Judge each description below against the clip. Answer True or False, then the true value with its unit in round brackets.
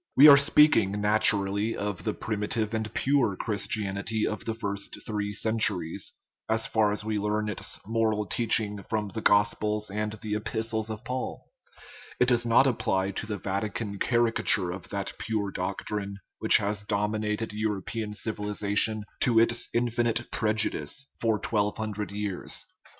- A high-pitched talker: False (105 Hz)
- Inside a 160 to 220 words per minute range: False (150 wpm)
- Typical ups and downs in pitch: False (1.7 semitones)